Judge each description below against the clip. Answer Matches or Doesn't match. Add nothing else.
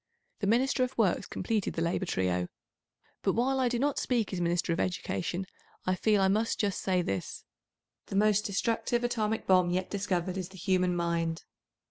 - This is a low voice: Doesn't match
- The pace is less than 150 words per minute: Doesn't match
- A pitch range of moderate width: Matches